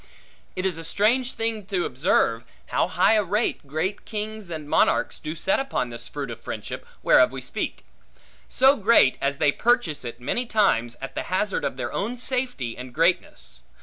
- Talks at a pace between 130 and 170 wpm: No, average, 180 wpm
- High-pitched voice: No, medium, 180 Hz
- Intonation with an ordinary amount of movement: No, wide, 8.5 semitones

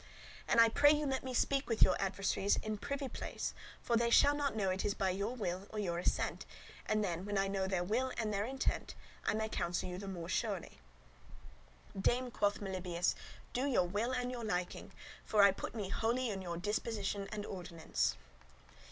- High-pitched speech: Yes, high, 205 Hz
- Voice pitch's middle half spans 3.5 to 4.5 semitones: Yes, average, 3.9 semitones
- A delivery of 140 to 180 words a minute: No, average, 195 wpm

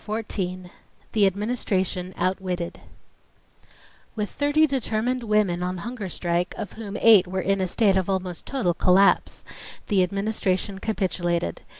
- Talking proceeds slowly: Yes, slow, 130 wpm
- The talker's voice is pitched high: Yes, high, 195 Hz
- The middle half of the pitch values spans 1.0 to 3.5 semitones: Yes, average, 3.0 semitones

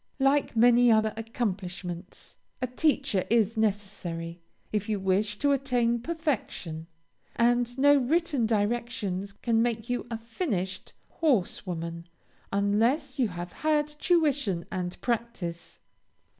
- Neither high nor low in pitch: No, high, 225 Hz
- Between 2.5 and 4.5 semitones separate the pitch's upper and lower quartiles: No, average, 5.1 semitones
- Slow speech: Yes, slow, 115 wpm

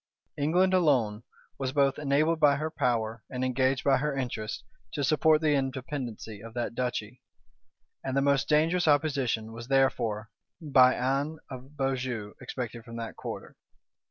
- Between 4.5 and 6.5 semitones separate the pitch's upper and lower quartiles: No, average, 3.6 semitones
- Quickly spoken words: No, average, 150 wpm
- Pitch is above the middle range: No, low, 135 Hz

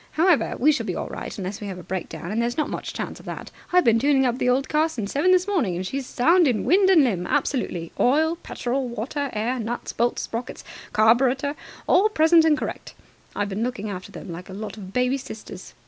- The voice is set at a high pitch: Yes, very high, 250 Hz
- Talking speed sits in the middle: No, fast, 225 wpm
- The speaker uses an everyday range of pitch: No, wide, 6.2 semitones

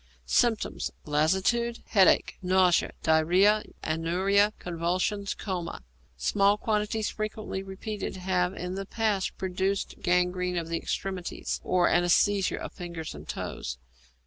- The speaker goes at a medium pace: No, slow, 115 wpm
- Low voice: No, medium, 185 Hz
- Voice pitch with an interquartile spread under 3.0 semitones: Yes, narrow, 2.5 semitones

